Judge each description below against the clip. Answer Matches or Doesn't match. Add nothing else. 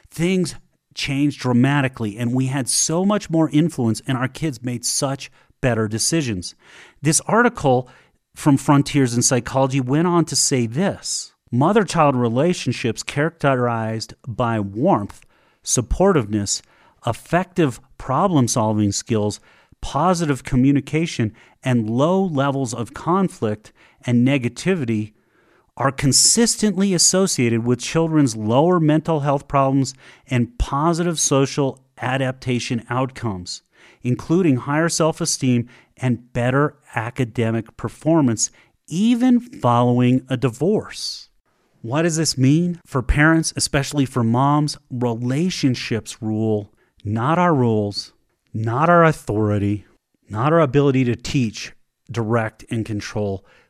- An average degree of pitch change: Matches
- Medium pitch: Doesn't match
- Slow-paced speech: Matches